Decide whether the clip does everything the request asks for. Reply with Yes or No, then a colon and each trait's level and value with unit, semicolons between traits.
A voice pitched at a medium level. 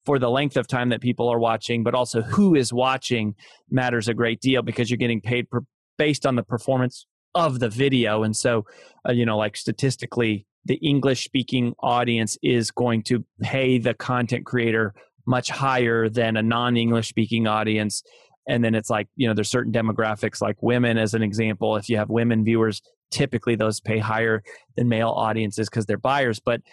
No: low, 120 Hz